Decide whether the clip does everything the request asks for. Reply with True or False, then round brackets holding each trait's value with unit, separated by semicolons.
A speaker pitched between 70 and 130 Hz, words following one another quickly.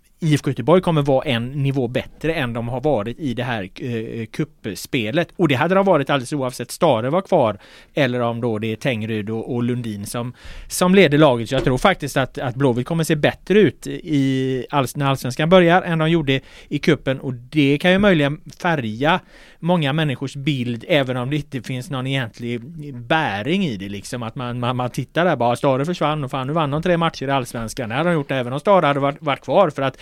False (140 Hz; 220 wpm)